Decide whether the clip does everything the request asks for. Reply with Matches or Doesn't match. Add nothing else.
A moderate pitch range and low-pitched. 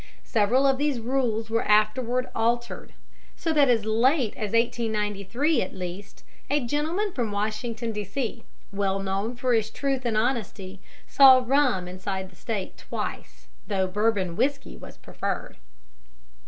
Doesn't match